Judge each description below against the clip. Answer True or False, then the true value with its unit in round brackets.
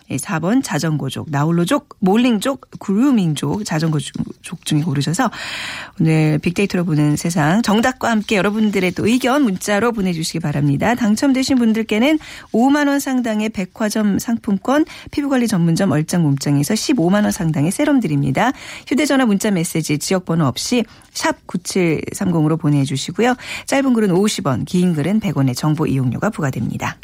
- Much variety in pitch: True (6.9 semitones)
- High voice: True (195 Hz)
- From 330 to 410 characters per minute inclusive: True (335 characters per minute)